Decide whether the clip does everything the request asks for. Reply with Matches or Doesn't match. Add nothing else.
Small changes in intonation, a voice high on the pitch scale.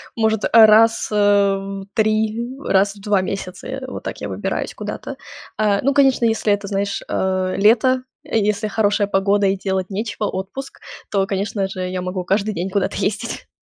Matches